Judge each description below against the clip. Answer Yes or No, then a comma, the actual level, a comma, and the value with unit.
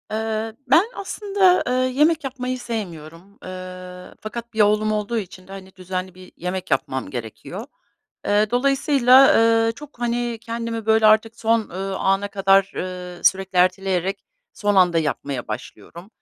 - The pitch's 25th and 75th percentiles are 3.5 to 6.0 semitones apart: Yes, average, 4.3 semitones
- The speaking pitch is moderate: No, high, 205 Hz